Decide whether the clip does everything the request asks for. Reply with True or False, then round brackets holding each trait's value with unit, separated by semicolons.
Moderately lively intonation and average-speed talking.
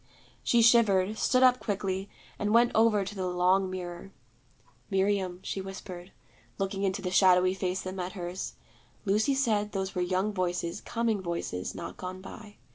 False (2.3 semitones; 160 wpm)